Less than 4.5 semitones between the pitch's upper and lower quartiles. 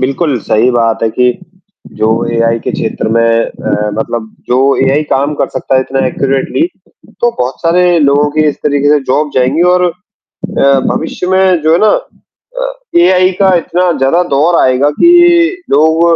No: average, 5.2 semitones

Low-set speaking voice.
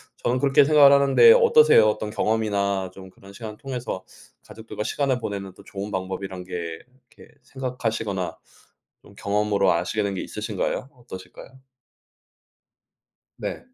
Yes: low, 105 Hz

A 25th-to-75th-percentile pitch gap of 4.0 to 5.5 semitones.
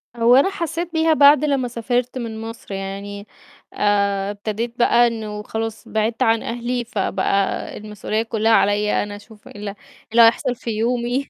No: average, 2.7 semitones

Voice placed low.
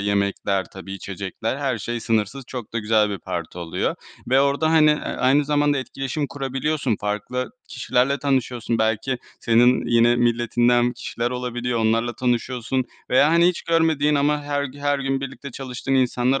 Yes: low, 125 Hz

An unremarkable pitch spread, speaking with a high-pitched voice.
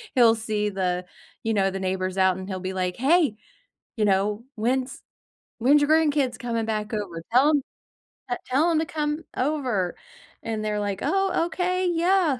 No: wide, 7.3 semitones; high, 230 Hz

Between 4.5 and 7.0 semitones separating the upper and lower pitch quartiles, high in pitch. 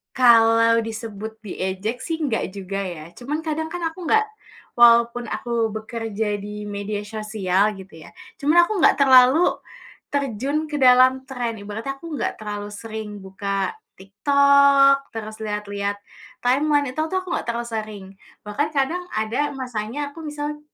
Yes: average, 5.2 semitones; high, 230 Hz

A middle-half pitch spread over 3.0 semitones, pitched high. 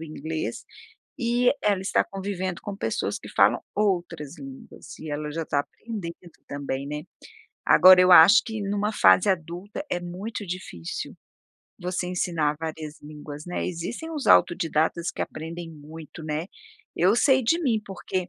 No: average, 4.3 semitones; medium, 175 Hz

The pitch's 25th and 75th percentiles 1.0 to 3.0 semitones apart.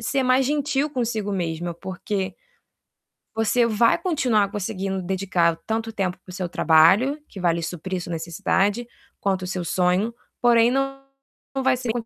No: average, 5.0 semitones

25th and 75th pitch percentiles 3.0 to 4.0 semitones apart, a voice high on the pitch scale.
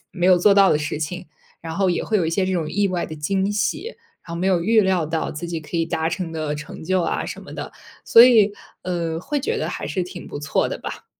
No: average, 3.3 semitones; medium, 180 Hz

